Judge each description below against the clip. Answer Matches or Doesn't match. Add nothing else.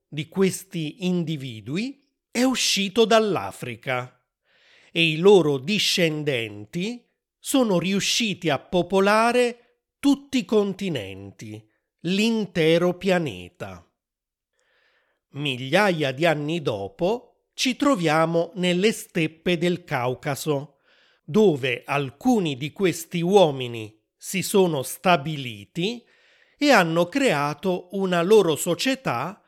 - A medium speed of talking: Doesn't match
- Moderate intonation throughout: Doesn't match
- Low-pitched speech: Doesn't match